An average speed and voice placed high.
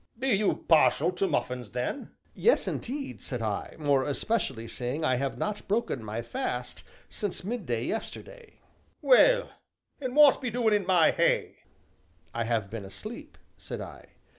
No: average, 150 wpm; medium, 165 Hz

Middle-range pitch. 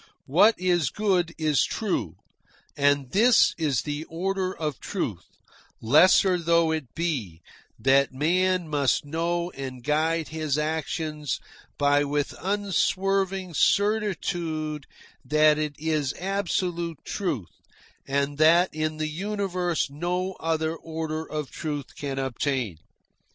Yes: medium, 160 Hz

